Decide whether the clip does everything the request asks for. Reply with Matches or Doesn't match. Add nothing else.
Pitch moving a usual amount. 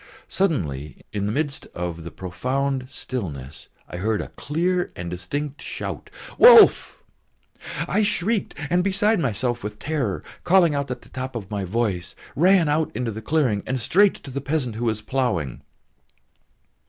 Doesn't match